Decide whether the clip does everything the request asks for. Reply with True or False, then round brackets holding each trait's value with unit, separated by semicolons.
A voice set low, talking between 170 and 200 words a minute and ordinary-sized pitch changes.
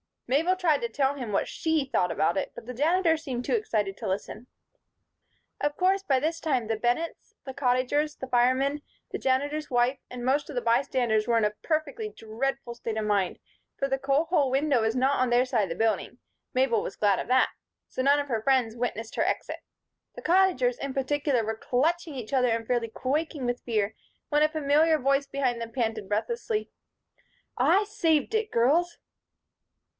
False (260 Hz; 190 wpm; 4.3 semitones)